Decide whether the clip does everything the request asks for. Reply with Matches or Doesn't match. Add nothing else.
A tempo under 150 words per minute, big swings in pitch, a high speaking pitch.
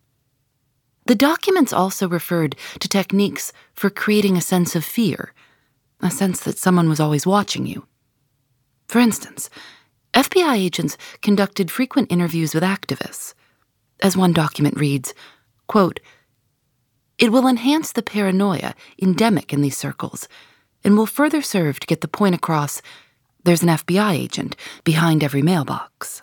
Doesn't match